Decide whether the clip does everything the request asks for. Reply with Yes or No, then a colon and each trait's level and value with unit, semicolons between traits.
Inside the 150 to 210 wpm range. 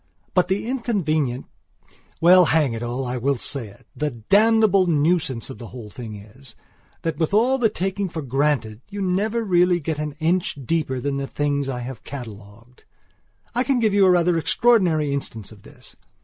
Yes: average, 175 wpm